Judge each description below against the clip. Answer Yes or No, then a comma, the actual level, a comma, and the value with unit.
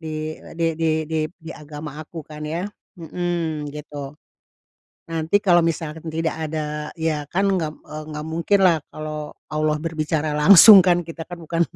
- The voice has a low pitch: No, medium, 160 Hz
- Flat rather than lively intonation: Yes, narrow, 1.8 semitones